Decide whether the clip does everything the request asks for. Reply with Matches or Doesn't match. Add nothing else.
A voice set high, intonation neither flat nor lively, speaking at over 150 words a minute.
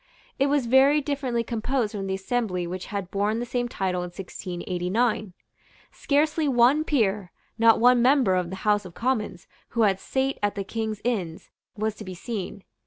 Matches